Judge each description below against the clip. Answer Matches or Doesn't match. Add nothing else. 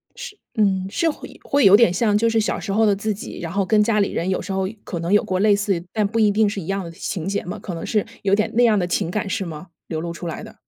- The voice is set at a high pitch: Matches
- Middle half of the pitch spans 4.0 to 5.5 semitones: Doesn't match